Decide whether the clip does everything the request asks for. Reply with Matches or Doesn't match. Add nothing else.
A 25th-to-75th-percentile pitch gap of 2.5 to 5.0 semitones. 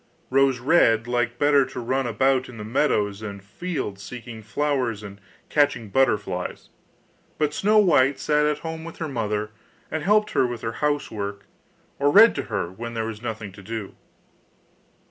Doesn't match